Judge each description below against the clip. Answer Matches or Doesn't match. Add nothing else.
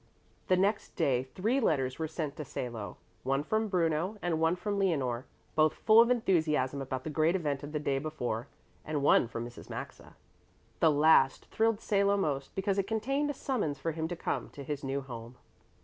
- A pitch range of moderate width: Doesn't match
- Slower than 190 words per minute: Doesn't match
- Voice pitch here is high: Doesn't match